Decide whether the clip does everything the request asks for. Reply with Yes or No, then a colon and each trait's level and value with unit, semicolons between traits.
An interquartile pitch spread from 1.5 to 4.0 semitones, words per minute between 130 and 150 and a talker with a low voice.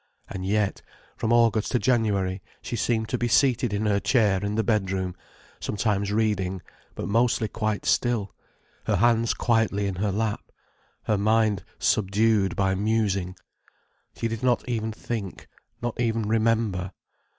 Yes: narrow, 2.4 semitones; average, 145 wpm; low, 110 Hz